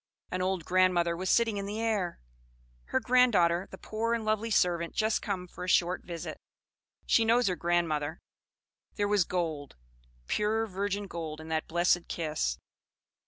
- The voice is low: No, medium, 185 Hz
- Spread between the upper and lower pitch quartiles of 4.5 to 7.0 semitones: No, average, 4.1 semitones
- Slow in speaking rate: No, average, 165 wpm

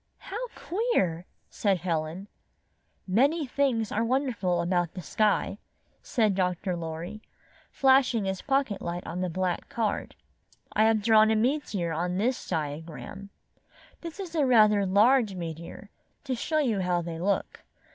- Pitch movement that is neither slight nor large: No, wide, 6.1 semitones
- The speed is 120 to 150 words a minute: Yes, average, 140 wpm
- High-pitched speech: Yes, high, 205 Hz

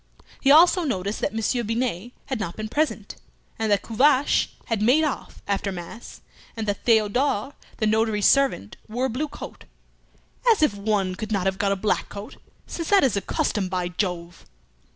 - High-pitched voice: Yes, high, 215 Hz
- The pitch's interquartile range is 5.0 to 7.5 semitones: No, average, 4.6 semitones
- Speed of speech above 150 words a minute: Yes, average, 180 wpm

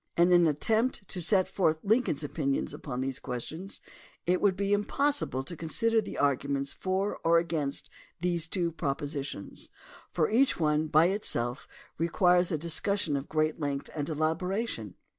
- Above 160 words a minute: No, average, 150 wpm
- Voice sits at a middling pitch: Yes, medium, 165 Hz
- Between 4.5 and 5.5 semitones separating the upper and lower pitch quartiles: Yes, average, 4.8 semitones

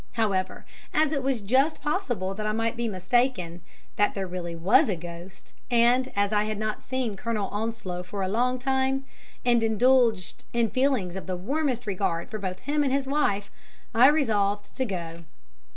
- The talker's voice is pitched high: Yes, high, 220 Hz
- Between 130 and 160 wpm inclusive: No, average, 180 wpm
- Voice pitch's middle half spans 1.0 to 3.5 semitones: No, average, 5.2 semitones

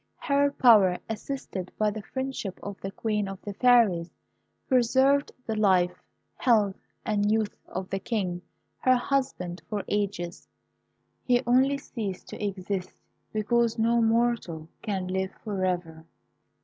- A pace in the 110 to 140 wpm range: Yes, slow, 135 wpm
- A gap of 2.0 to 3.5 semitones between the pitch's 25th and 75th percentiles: No, average, 4.2 semitones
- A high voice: Yes, high, 210 Hz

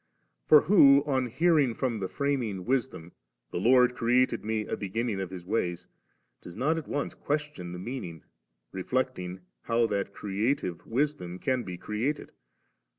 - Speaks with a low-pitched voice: Yes, low, 115 Hz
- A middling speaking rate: Yes, average, 150 wpm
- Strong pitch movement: Yes, wide, 6.3 semitones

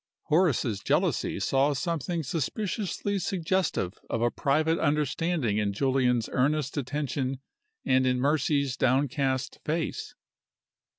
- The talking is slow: Yes, slow, 105 wpm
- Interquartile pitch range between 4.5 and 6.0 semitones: No, average, 4.0 semitones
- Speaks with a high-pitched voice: No, medium, 140 Hz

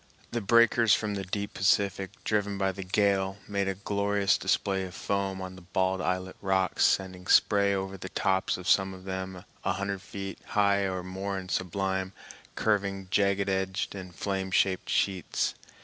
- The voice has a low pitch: Yes, very low, 95 Hz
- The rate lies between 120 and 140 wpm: No, average, 170 wpm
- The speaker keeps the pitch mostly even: Yes, narrow, 1.0 semitones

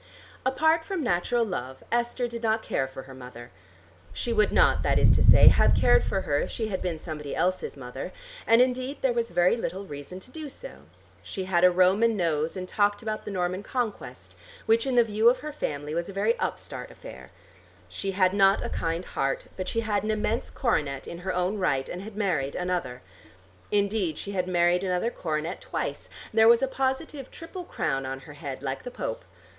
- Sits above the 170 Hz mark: Yes, high, 190 Hz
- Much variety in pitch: Yes, wide, 5.9 semitones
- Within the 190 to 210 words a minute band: Yes, fast, 205 wpm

